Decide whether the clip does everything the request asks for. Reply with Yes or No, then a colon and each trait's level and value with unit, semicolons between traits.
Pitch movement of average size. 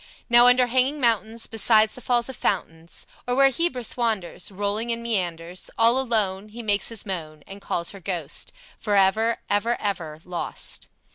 Yes: average, 3.9 semitones